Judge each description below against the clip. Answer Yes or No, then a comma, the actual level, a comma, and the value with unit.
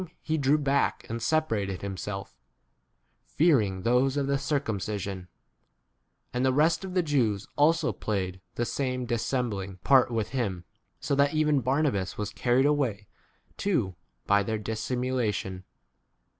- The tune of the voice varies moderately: No, wide, 5.7 semitones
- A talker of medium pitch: No, low, 125 Hz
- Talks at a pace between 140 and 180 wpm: Yes, average, 145 wpm